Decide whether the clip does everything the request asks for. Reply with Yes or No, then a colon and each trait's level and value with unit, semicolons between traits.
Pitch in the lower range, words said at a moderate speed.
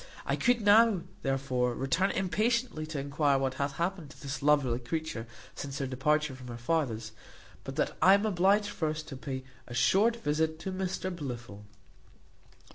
No: medium, 150 Hz; average, 165 wpm